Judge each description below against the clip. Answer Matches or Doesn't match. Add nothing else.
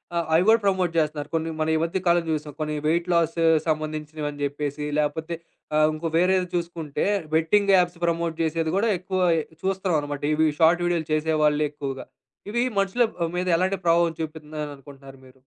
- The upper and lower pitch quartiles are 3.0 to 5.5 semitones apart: Doesn't match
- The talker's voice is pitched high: Doesn't match